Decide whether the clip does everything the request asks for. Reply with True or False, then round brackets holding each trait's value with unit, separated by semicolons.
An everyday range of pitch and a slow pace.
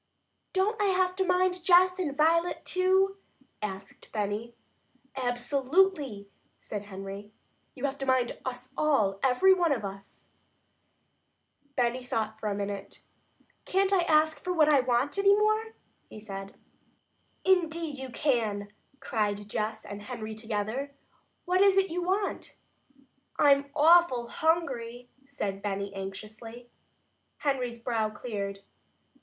False (8.4 semitones; 125 wpm)